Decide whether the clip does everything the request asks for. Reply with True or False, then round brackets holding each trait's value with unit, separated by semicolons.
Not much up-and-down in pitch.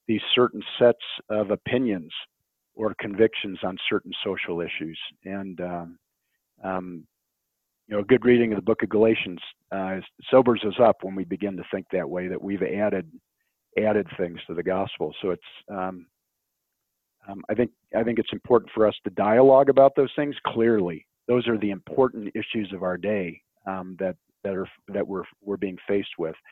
False (3.6 semitones)